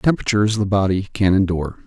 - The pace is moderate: Yes, average, 160 wpm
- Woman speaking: No, male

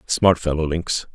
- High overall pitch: No, very low, 80 Hz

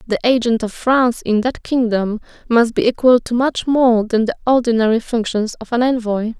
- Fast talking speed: No, average, 190 wpm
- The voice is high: Yes, high, 235 Hz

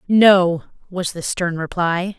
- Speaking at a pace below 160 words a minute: Yes, slow, 135 wpm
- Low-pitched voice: No, medium, 180 Hz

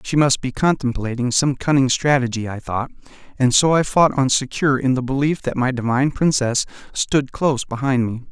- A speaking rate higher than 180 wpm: Yes, average, 190 wpm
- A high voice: No, low, 135 Hz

